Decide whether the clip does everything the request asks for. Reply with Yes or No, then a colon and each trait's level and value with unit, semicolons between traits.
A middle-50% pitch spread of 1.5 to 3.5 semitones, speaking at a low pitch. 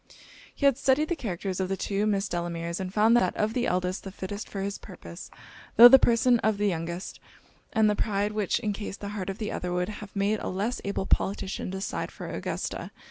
No: narrow, 2.6 semitones; high, 200 Hz